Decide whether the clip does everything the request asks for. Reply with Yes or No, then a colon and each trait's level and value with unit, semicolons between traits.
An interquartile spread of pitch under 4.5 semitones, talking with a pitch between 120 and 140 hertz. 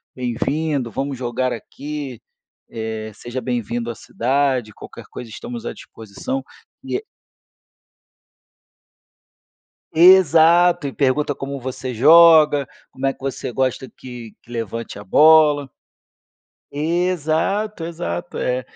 No: average, 4.8 semitones; low, 135 Hz